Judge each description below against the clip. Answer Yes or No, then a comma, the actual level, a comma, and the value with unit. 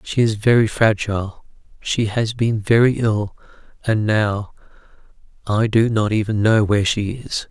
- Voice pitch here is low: Yes, low, 110 Hz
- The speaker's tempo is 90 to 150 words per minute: Yes, average, 145 wpm